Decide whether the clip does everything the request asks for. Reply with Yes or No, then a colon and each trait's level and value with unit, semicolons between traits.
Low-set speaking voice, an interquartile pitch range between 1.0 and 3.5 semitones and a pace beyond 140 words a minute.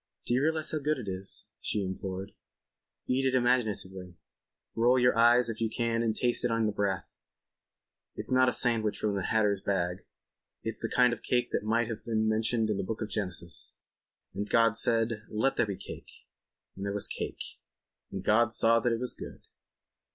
Yes: low, 110 Hz; average, 3.1 semitones; average, 190 wpm